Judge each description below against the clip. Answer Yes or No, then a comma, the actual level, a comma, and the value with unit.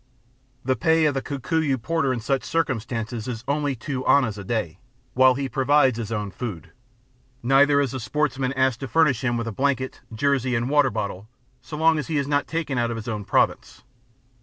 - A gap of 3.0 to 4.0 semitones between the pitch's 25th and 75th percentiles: Yes, average, 3.7 semitones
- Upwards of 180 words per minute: Yes, average, 200 wpm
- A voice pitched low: Yes, low, 130 Hz